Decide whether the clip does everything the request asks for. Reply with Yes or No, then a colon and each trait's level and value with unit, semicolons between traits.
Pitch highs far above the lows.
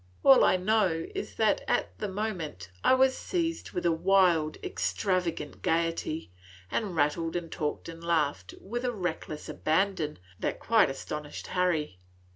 No: average, 4.6 semitones